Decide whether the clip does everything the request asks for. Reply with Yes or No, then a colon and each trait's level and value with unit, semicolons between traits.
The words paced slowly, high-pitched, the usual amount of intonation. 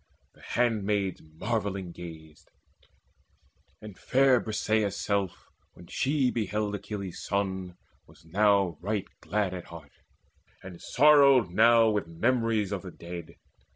No: slow, 120 wpm; low, 100 Hz; average, 3.9 semitones